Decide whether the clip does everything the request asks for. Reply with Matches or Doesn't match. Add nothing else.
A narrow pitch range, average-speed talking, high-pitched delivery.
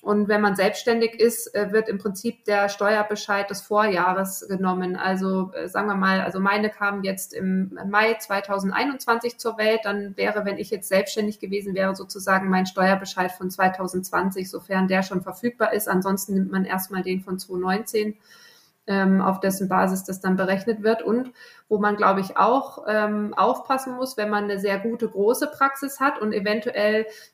Matches